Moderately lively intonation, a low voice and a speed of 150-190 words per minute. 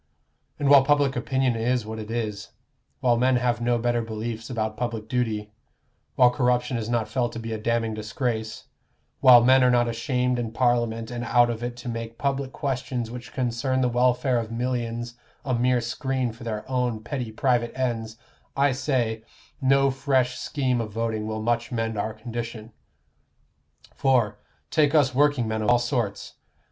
No: narrow, 1.9 semitones; low, 120 Hz; average, 170 wpm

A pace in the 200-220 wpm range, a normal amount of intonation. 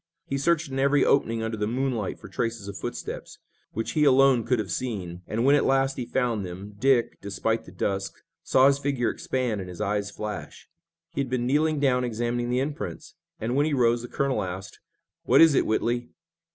Yes: fast, 205 wpm; average, 4.1 semitones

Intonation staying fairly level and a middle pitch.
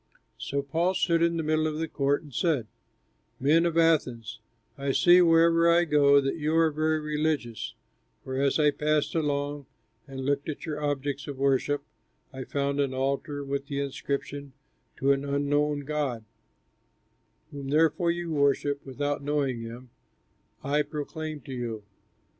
Yes: narrow, 2.2 semitones; medium, 145 Hz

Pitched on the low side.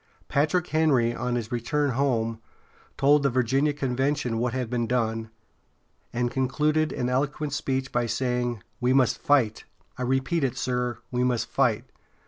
Yes: low, 125 Hz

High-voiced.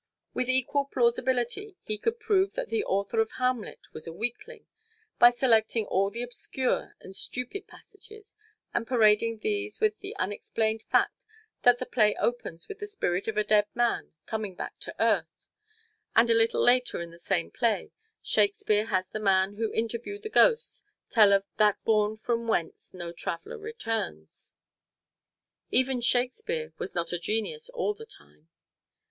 Yes: high, 230 Hz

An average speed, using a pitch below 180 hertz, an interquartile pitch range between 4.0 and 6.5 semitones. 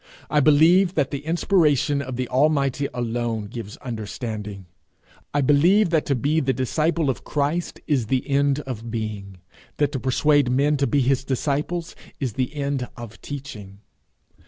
No: average, 160 wpm; medium, 140 Hz; average, 3.6 semitones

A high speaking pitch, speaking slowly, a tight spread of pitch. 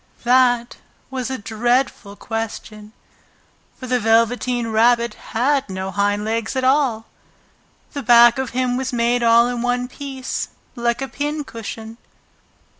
Yes: high, 240 Hz; slow, 130 wpm; narrow, 2.3 semitones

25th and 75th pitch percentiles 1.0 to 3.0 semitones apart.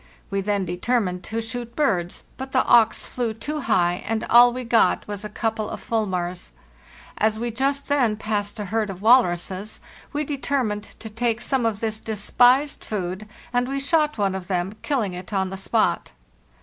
No: average, 3.9 semitones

